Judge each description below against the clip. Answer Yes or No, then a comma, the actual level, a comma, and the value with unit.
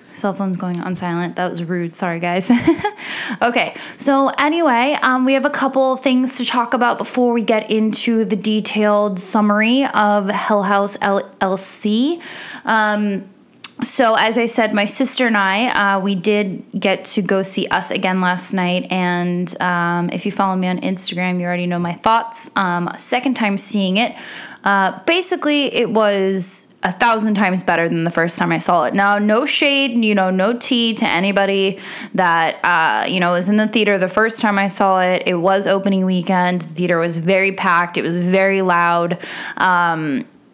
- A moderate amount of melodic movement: Yes, average, 4.0 semitones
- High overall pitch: Yes, high, 200 Hz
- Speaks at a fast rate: No, average, 180 wpm